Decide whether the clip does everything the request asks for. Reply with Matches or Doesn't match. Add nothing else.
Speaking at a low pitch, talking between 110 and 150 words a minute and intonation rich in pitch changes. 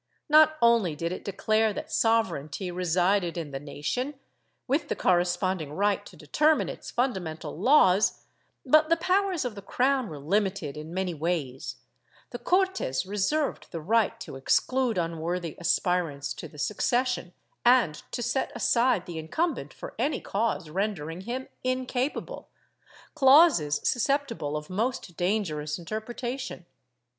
Doesn't match